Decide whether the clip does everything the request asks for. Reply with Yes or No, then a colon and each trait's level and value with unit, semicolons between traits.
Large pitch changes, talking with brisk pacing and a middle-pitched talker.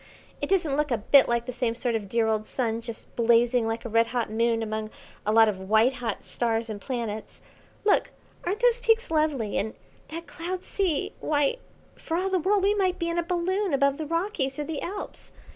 No: wide, 7.1 semitones; fast, 210 wpm; very high, 265 Hz